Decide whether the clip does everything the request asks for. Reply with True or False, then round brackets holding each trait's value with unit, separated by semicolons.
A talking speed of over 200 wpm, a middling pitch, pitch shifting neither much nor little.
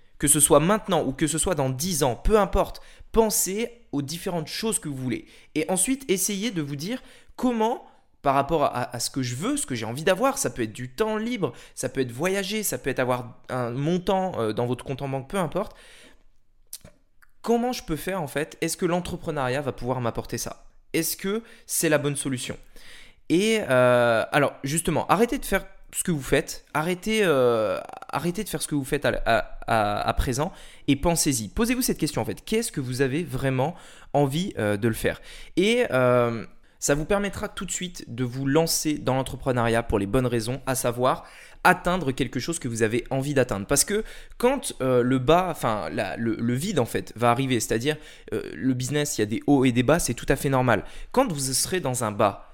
False (215 wpm; 145 Hz; 6.5 semitones)